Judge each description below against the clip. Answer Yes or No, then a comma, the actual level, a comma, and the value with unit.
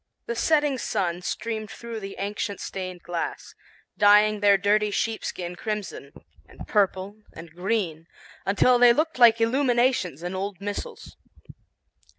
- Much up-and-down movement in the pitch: No, average, 3.7 semitones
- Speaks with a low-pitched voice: No, high, 205 Hz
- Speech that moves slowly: Yes, slow, 130 wpm